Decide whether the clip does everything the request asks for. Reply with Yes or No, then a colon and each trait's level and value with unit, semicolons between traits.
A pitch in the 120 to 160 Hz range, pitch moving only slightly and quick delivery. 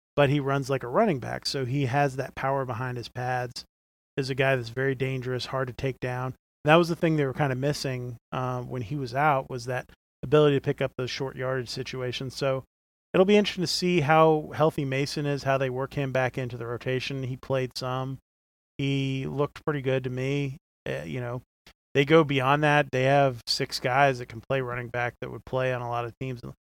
Yes: low, 135 Hz; narrow, 1.9 semitones; fast, 225 wpm